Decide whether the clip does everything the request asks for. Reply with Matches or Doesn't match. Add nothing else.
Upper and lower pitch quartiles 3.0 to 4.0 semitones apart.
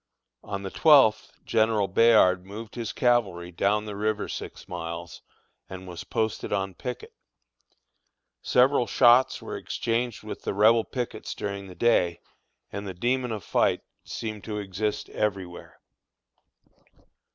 Matches